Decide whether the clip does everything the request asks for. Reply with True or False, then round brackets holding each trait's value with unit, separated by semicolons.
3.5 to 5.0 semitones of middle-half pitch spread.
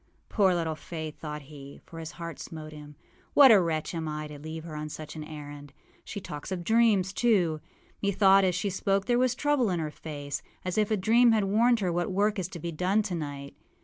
True (4.7 semitones)